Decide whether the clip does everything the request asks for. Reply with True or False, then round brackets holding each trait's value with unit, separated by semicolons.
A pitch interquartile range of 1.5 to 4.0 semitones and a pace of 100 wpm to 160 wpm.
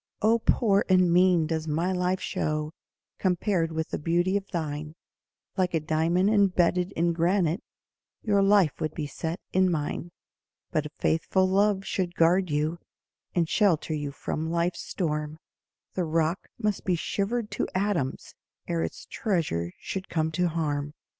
True (3.2 semitones; 155 wpm)